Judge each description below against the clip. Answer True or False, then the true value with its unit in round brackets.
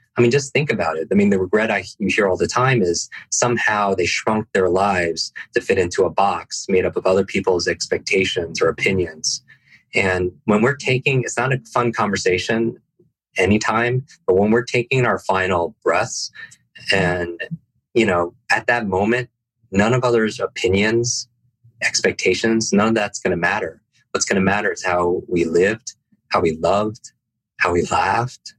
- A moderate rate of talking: True (170 wpm)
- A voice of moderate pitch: False (115 Hz)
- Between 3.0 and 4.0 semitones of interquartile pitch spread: True (3.6 semitones)